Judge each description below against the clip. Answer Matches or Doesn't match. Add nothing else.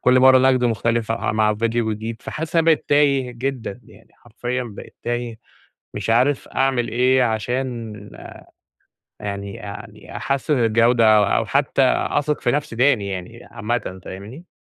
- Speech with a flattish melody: Doesn't match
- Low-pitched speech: Matches